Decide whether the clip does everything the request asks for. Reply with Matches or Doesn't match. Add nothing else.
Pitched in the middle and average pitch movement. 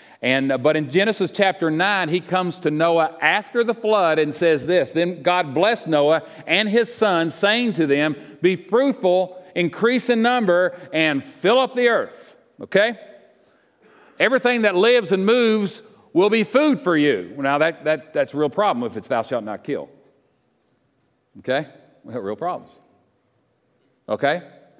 Doesn't match